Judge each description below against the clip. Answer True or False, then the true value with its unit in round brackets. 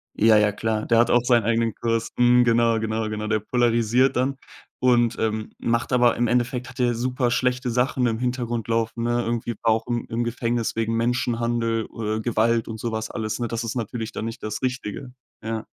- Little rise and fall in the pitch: True (1.5 semitones)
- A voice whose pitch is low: True (115 Hz)